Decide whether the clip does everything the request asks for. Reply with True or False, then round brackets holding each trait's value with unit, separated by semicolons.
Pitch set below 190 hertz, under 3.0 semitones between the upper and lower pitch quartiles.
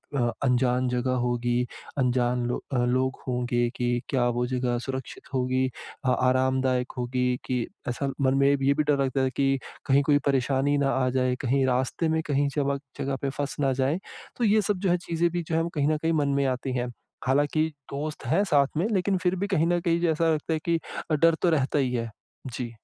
False (135 Hz; 3.4 semitones)